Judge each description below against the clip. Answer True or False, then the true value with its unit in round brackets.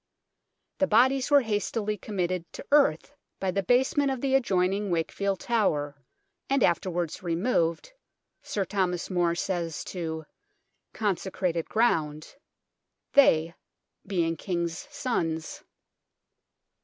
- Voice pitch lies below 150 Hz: False (185 Hz)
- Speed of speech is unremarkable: False (105 wpm)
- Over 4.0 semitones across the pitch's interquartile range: True (5.1 semitones)